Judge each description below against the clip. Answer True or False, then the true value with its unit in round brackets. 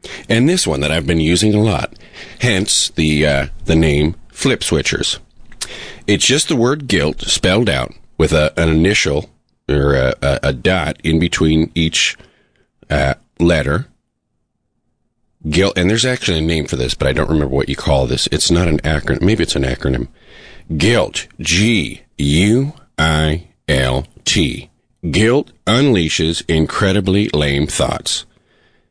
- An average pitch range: True (3.8 semitones)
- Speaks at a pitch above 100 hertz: False (80 Hz)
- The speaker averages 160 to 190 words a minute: False (150 wpm)